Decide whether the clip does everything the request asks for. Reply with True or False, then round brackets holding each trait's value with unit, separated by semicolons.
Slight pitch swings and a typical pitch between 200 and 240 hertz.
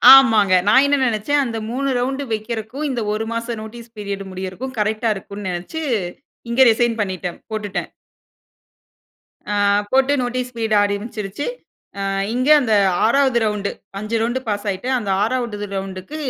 False (3.6 semitones; 225 Hz)